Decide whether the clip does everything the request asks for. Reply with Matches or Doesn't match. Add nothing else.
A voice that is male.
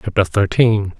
Matches